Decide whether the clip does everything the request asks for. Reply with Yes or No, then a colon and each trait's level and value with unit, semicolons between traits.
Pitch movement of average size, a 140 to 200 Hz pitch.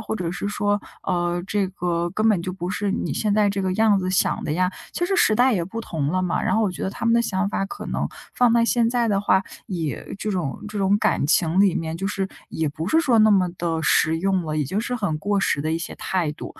Yes: average, 3.5 semitones; high, 190 Hz